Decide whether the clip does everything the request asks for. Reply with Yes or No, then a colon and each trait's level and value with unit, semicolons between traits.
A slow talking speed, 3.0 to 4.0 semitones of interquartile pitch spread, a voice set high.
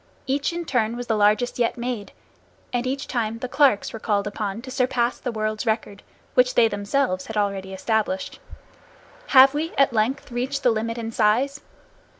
No: average, 175 wpm; average, 3.4 semitones; high, 235 Hz